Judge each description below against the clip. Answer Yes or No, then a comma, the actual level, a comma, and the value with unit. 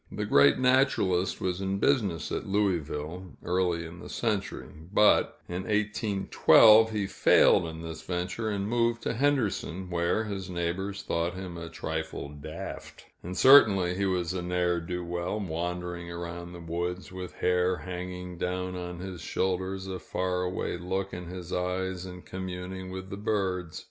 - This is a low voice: Yes, very low, 90 Hz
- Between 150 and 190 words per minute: Yes, average, 160 wpm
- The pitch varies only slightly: Yes, narrow, 1.8 semitones